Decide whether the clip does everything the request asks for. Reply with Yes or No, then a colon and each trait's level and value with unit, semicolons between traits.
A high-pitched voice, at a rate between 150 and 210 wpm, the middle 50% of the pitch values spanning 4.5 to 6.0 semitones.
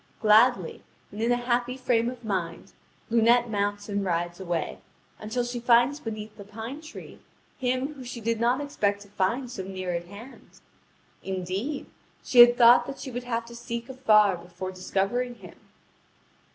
No: high, 230 Hz; average, 165 wpm; average, 3.6 semitones